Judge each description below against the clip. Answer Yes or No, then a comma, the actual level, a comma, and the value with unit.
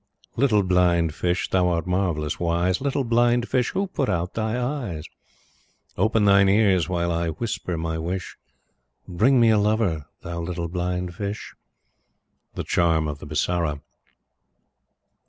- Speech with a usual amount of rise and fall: Yes, average, 4.4 semitones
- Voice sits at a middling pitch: No, very low, 90 Hz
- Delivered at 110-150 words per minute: Yes, average, 140 wpm